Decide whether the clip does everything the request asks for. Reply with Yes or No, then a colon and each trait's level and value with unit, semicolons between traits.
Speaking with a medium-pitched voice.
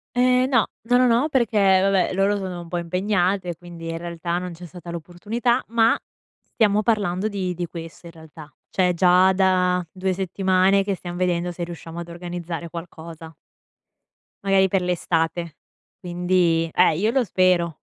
Yes: medium, 180 Hz